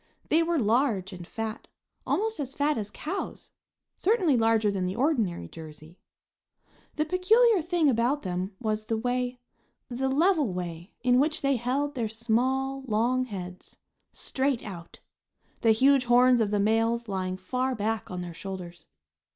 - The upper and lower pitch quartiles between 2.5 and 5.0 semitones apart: No, wide, 5.5 semitones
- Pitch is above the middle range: Yes, high, 235 Hz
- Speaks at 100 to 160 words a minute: Yes, average, 150 wpm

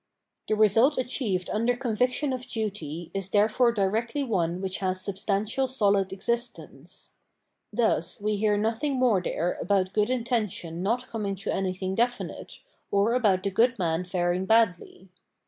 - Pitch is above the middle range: Yes, high, 205 Hz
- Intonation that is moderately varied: Yes, average, 4.0 semitones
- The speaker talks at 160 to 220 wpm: No, average, 150 wpm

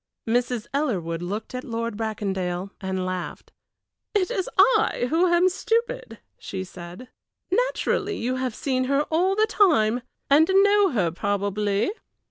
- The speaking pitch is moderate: No, high, 245 Hz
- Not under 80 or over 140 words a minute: Yes, slow, 135 wpm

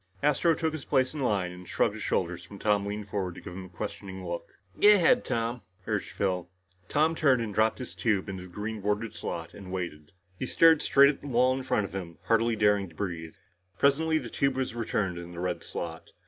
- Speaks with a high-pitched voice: No, low, 105 Hz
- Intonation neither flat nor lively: No, wide, 6.1 semitones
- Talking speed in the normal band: No, fast, 225 wpm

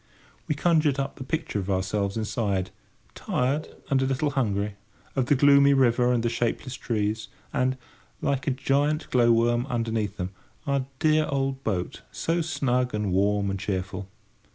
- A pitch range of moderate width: Yes, average, 4.8 semitones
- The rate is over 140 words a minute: Yes, average, 160 wpm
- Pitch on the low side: Yes, low, 125 Hz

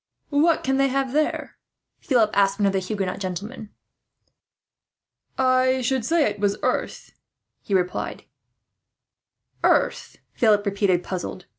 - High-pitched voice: Yes, high, 215 Hz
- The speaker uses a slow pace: Yes, slow, 125 wpm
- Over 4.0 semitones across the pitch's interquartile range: Yes, average, 5.0 semitones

